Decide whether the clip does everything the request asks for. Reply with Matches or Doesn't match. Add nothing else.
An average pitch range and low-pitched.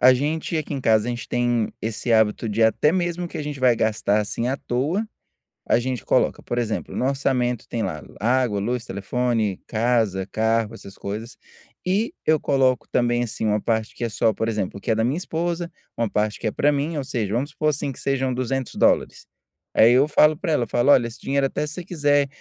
Matches